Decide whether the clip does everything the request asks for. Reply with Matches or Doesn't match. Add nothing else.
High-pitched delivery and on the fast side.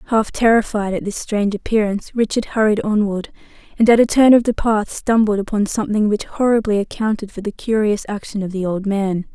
Doesn't match